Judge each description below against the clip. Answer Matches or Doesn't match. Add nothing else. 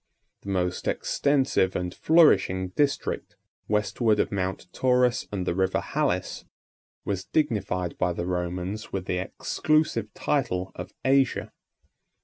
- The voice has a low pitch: Matches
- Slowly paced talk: Matches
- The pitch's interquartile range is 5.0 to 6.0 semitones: Matches